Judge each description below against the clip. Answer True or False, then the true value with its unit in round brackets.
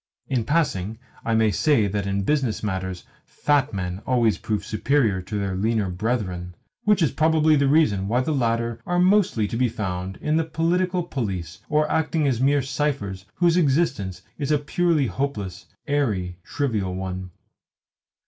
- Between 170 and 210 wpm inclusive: False (160 wpm)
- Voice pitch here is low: True (115 Hz)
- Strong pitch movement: True (7.3 semitones)